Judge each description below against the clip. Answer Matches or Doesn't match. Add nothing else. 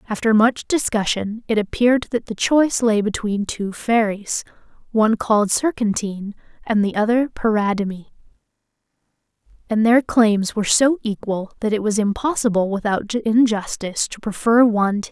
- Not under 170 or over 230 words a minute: Doesn't match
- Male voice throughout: Doesn't match